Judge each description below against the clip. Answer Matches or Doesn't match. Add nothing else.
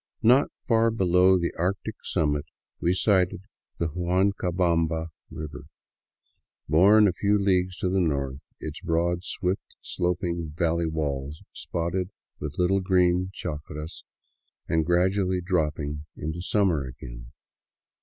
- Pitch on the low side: Matches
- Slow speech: Matches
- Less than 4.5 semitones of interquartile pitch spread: Matches